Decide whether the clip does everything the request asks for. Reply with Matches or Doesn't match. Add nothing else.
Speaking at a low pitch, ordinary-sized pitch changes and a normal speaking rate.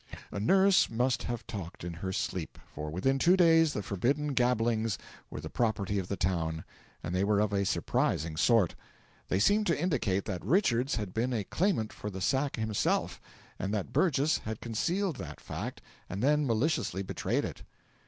Doesn't match